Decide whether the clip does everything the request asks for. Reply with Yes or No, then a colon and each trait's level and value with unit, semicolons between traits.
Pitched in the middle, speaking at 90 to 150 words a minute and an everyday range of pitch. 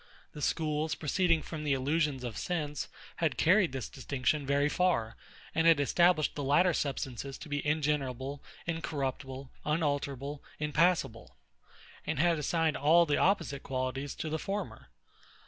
Yes: medium, 150 Hz; average, 140 wpm; average, 3.1 semitones